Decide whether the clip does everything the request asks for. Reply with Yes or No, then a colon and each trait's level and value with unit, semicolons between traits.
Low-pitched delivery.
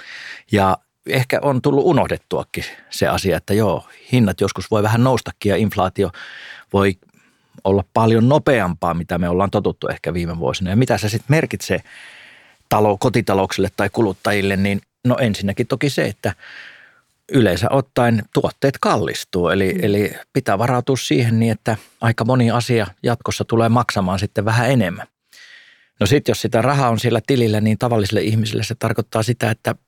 Yes: low, 115 Hz